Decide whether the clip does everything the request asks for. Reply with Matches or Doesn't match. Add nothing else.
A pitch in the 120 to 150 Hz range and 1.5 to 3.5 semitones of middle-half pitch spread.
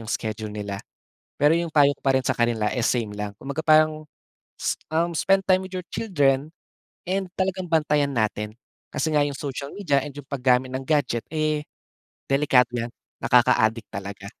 Doesn't match